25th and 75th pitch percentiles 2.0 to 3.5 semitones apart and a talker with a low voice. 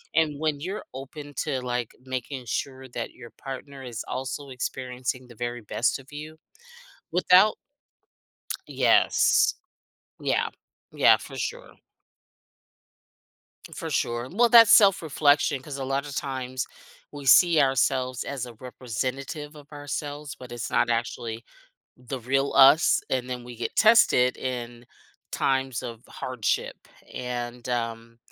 Yes: average, 3.0 semitones; low, 130 Hz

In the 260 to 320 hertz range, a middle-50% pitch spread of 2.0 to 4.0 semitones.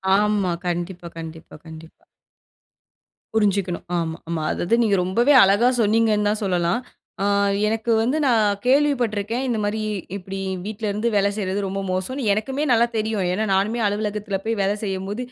No: high, 205 Hz; average, 2.9 semitones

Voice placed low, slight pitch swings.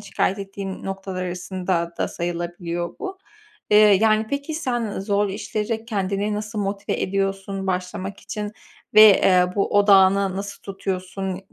No: high, 195 Hz; narrow, 1.9 semitones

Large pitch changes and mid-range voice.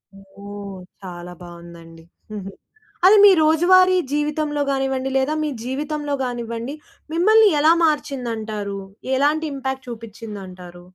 No: wide, 7.0 semitones; very high, 255 Hz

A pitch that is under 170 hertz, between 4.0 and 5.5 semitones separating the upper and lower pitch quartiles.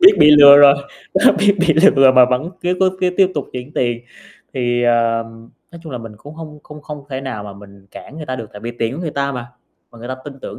Yes: low, 135 Hz; average, 4.3 semitones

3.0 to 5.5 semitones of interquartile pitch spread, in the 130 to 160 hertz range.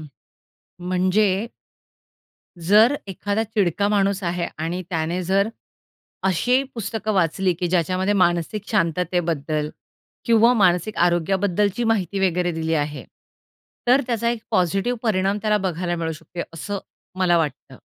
No: average, 3.5 semitones; medium, 185 Hz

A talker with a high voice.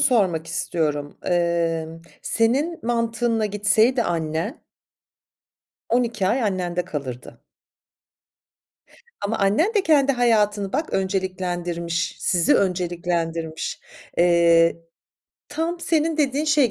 Yes: high, 195 Hz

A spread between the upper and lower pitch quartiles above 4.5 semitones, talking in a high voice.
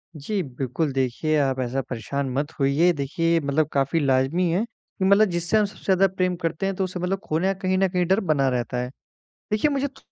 No: wide, 5.5 semitones; medium, 165 Hz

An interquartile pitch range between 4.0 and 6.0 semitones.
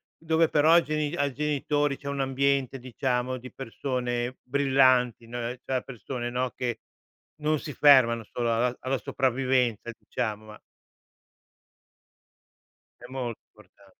No: narrow, 2.5 semitones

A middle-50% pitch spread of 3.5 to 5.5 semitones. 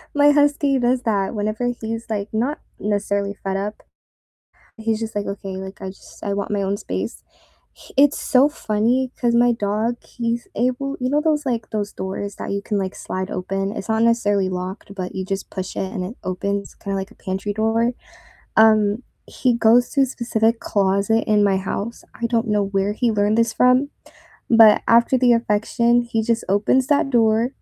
No: average, 3.1 semitones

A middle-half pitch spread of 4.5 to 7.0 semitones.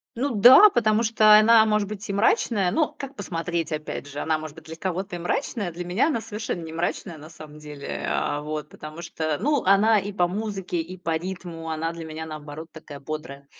Yes: average, 5.1 semitones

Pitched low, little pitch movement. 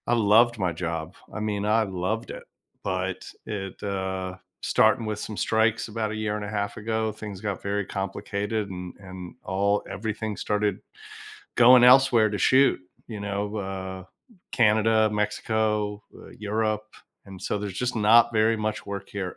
Yes: low, 105 Hz; narrow, 2.1 semitones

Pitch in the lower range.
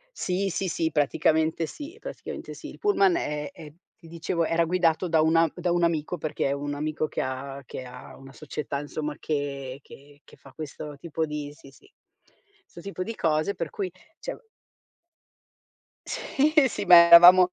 No: medium, 160 Hz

